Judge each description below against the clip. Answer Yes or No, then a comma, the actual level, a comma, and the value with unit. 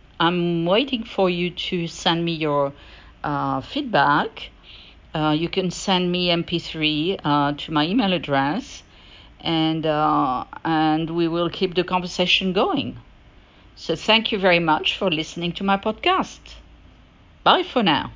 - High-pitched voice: No, medium, 170 Hz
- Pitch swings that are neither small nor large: Yes, average, 3.4 semitones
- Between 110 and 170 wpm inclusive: Yes, average, 140 wpm